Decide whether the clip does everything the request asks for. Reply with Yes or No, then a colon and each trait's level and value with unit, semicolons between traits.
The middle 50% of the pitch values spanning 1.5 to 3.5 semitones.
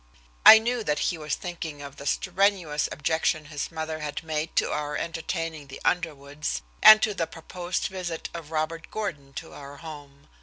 Yes: average, 2.9 semitones